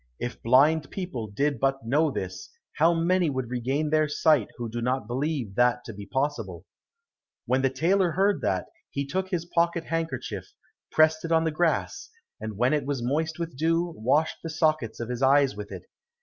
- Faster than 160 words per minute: Yes, average, 190 wpm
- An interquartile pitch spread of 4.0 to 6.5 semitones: Yes, average, 4.9 semitones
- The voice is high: No, medium, 145 Hz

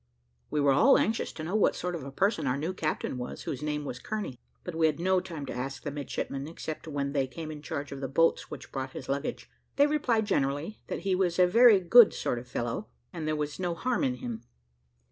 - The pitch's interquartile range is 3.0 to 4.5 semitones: No, average, 5.0 semitones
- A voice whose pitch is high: No, medium, 155 Hz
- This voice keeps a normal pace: No, fast, 240 wpm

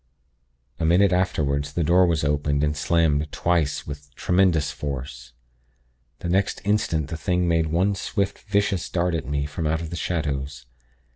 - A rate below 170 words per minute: Yes, average, 160 wpm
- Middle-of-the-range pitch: No, very low, 80 Hz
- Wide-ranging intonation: No, average, 3.5 semitones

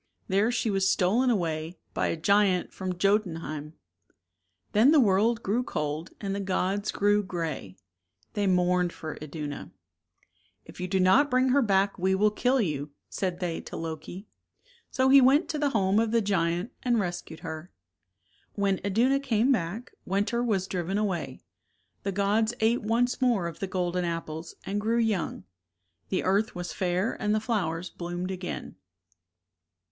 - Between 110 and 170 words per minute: Yes, average, 165 wpm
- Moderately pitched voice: No, high, 195 Hz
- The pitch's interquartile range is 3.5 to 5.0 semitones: Yes, average, 4.0 semitones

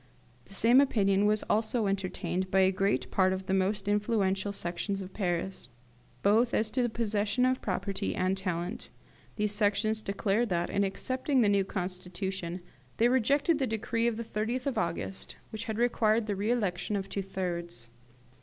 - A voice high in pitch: Yes, high, 205 Hz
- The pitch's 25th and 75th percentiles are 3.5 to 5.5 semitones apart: No, average, 3.0 semitones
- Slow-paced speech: No, average, 170 wpm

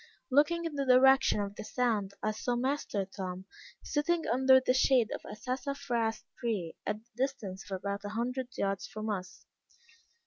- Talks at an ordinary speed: Yes, average, 170 wpm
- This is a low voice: No, high, 235 Hz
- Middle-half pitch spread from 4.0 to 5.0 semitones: Yes, average, 4.5 semitones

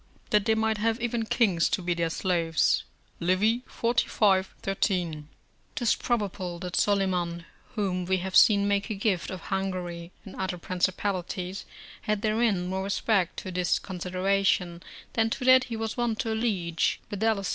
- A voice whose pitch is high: Yes, high, 195 Hz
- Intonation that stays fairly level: No, average, 3.5 semitones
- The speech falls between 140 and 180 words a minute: Yes, average, 155 wpm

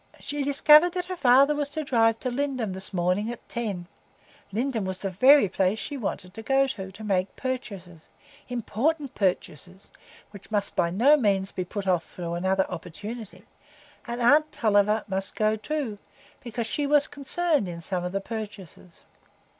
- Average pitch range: No, wide, 6.2 semitones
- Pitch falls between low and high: No, high, 220 Hz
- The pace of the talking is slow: No, average, 165 wpm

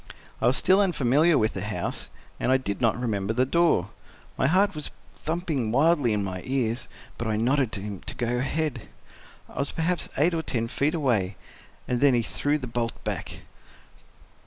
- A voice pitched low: Yes, low, 130 Hz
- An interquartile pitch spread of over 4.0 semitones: Yes, average, 5.1 semitones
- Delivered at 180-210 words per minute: Yes, average, 185 wpm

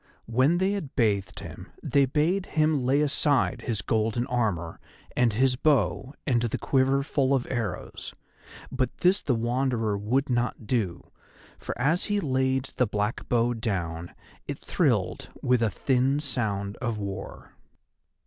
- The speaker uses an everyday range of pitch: Yes, average, 3.7 semitones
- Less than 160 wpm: Yes, average, 150 wpm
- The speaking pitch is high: No, low, 125 Hz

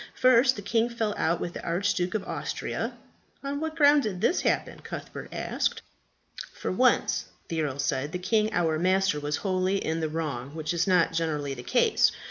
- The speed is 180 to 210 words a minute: Yes, average, 185 wpm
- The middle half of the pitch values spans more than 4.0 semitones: Yes, wide, 5.5 semitones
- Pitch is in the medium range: Yes, medium, 180 Hz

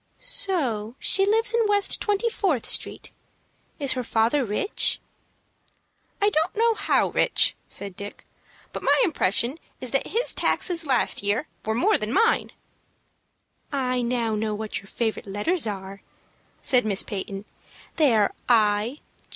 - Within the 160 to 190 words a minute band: No, average, 145 wpm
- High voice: Yes, very high, 250 Hz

